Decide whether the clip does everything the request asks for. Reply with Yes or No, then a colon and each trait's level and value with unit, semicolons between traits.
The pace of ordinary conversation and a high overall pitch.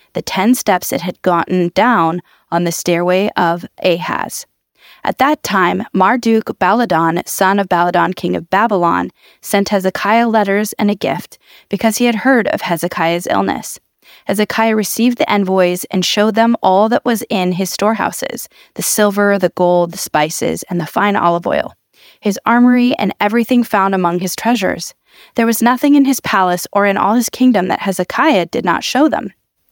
Yes: average, 170 wpm; high, 200 Hz